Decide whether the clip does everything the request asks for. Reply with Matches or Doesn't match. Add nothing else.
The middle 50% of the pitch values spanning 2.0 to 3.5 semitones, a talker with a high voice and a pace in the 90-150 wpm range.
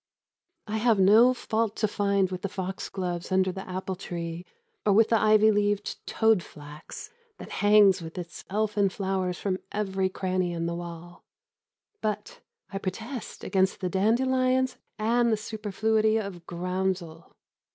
Matches